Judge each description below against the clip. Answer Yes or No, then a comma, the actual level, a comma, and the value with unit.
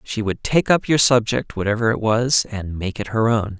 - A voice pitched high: No, low, 115 Hz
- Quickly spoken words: Yes, fast, 235 wpm